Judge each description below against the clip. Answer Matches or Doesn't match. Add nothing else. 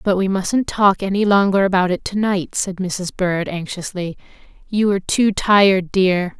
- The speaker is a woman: Matches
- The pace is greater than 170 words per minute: Matches